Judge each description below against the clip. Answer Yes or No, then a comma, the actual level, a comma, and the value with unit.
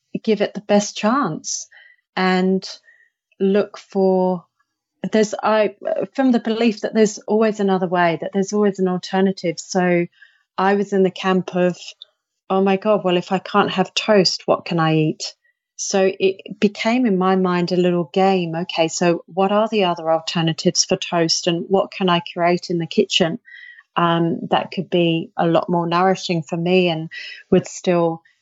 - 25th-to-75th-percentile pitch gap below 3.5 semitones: Yes, average, 2.8 semitones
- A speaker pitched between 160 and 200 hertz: Yes, high, 190 Hz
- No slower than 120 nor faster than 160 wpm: No, average, 175 wpm